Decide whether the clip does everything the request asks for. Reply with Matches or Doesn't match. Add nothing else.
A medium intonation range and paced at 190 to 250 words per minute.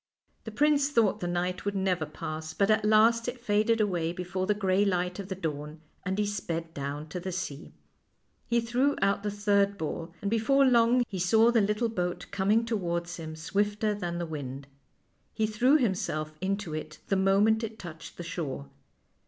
Matches